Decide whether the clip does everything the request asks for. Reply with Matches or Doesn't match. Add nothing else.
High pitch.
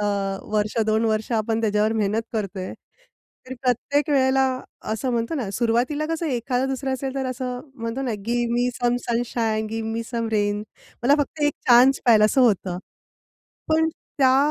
Matches